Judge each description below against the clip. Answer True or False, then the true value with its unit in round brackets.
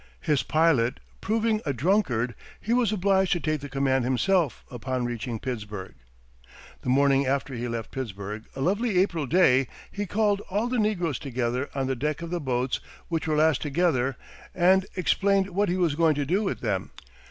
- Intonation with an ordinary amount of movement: False (6.8 semitones)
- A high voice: False (150 Hz)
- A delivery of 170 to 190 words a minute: True (180 wpm)